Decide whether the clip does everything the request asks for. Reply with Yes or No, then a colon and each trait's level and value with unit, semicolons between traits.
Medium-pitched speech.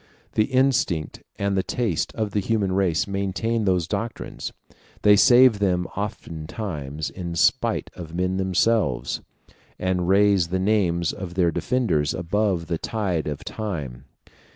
No: very low, 95 Hz